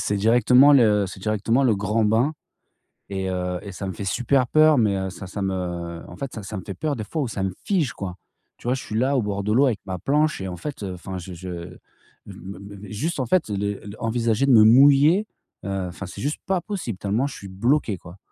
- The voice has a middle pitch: No, low, 105 Hz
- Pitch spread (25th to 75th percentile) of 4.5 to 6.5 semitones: Yes, wide, 5.6 semitones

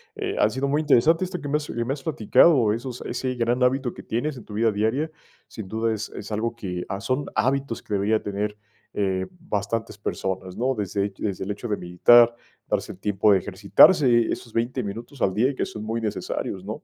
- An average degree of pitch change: Yes, average, 3.9 semitones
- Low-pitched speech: Yes, low, 115 Hz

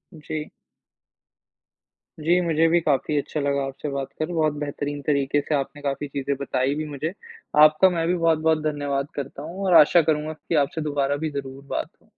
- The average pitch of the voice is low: No, medium, 150 Hz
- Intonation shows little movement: Yes, narrow, 2.1 semitones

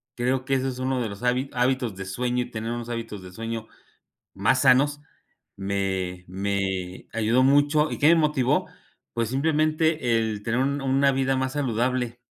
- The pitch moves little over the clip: No, average, 3.6 semitones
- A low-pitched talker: Yes, low, 125 Hz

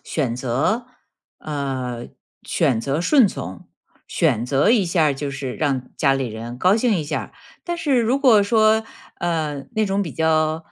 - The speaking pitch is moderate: Yes, medium, 155 Hz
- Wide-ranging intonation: Yes, wide, 8.0 semitones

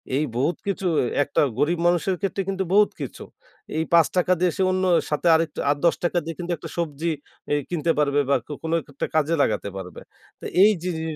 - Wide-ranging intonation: No, average, 3.4 semitones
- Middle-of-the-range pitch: Yes, medium, 165 Hz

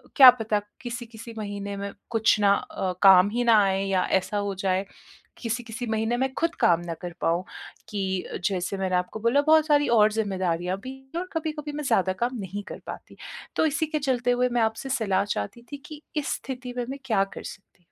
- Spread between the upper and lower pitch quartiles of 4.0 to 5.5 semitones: Yes, average, 4.7 semitones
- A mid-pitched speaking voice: No, high, 220 Hz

